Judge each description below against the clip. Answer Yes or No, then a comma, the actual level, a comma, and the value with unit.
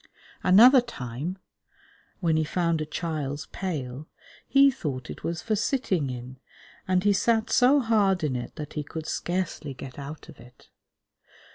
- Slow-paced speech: No, average, 155 wpm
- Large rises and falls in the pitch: Yes, wide, 6.1 semitones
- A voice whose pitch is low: No, medium, 165 Hz